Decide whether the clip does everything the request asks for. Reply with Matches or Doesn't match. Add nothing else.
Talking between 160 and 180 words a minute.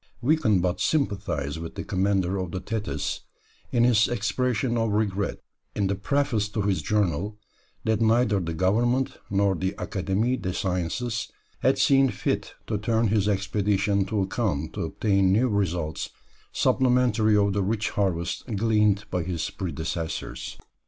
Doesn't match